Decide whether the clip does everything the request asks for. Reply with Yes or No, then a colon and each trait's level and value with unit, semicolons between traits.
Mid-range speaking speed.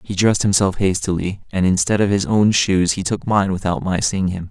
No: fast, 225 wpm